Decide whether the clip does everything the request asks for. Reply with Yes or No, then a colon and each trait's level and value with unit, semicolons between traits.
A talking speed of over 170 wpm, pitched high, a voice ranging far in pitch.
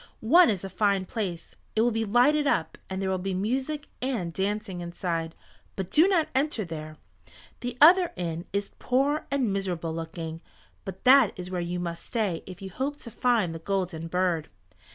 Yes: average, 185 wpm; high, 195 Hz; wide, 6.2 semitones